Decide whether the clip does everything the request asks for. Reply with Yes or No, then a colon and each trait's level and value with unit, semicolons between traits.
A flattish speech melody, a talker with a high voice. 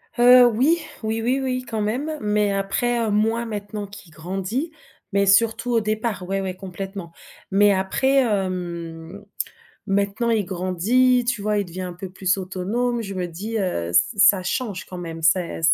No: average, 3.9 semitones; high, 205 Hz